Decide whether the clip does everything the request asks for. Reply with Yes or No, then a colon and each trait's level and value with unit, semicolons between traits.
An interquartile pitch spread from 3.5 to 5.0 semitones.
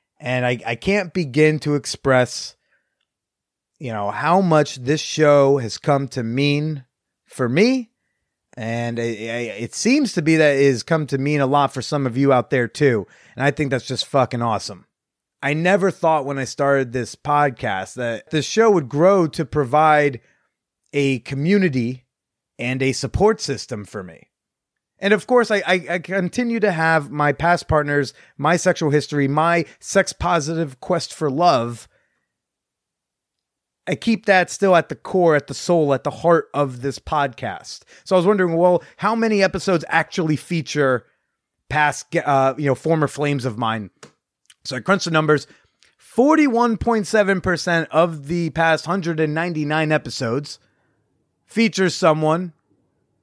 Yes: average, 4.7 semitones